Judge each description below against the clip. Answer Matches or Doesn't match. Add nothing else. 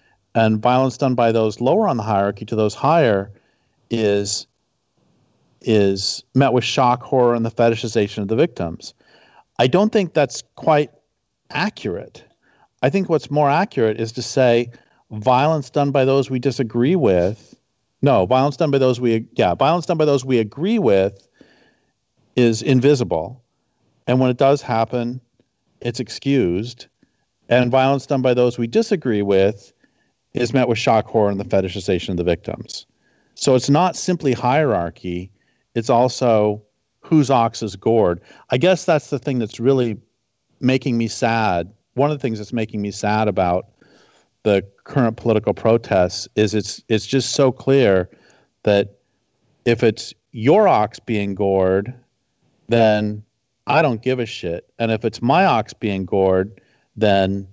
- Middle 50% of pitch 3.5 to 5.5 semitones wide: Matches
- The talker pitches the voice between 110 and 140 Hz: Matches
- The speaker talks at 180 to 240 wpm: Doesn't match